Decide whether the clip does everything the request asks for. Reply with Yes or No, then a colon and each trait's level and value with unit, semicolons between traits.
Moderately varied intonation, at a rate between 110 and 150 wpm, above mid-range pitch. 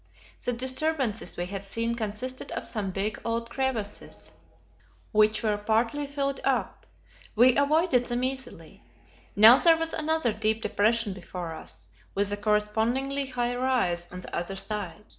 Yes: average, 4.0 semitones; average, 145 wpm; high, 230 Hz